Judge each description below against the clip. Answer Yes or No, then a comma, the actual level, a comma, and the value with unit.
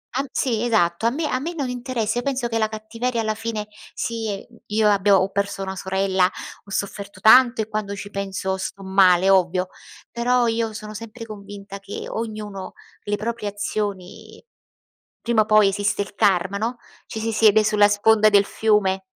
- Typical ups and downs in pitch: No, narrow, 2.3 semitones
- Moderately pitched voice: No, high, 215 Hz